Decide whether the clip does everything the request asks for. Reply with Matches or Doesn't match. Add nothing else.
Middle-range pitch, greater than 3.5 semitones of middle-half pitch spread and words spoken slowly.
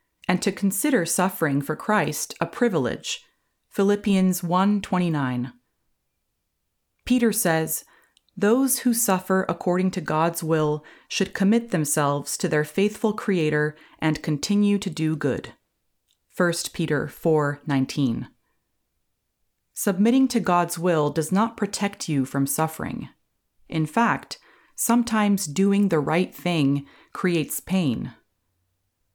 Matches